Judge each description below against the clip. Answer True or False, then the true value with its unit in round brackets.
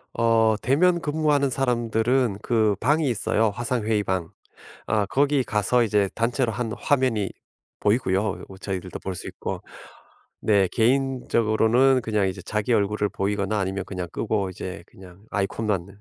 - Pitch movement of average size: True (4.0 semitones)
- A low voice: True (110 Hz)